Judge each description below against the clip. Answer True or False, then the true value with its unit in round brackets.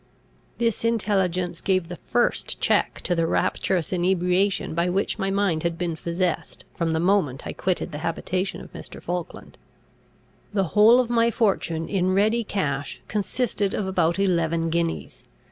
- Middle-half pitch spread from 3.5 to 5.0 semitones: False (3.1 semitones)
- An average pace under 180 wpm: True (155 wpm)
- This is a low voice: False (185 Hz)